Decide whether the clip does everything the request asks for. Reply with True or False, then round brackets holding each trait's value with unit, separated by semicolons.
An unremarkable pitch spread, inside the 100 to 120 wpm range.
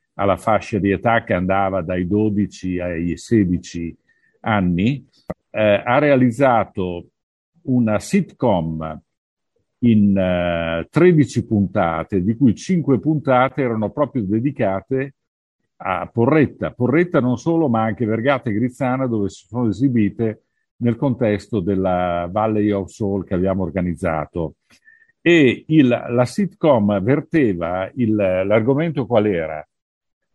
False (5.7 semitones; 115 wpm)